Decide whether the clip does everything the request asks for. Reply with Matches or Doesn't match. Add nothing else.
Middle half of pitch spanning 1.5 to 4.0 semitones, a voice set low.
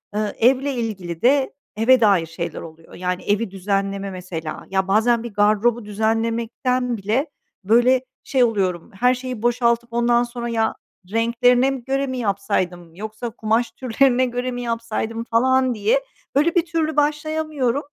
Doesn't match